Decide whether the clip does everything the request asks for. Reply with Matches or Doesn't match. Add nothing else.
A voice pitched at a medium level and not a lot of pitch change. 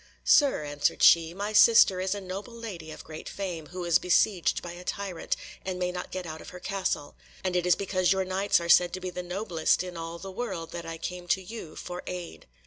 Matches